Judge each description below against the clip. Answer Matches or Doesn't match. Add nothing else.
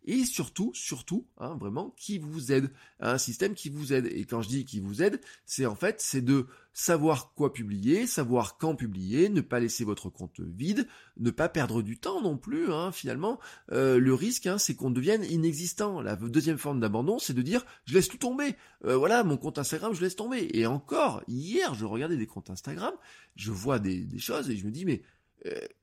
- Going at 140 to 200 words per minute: Doesn't match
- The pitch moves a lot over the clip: Matches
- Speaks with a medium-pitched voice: Matches